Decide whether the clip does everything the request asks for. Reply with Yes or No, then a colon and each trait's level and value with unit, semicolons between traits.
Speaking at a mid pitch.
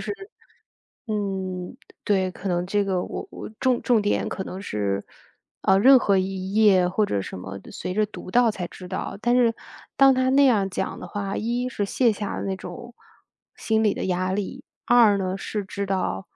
No: high, 200 Hz